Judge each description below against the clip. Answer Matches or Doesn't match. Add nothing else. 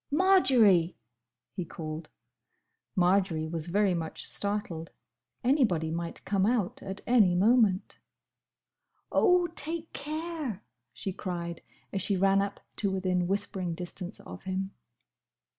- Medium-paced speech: Doesn't match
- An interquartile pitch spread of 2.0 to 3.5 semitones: Doesn't match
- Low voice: Doesn't match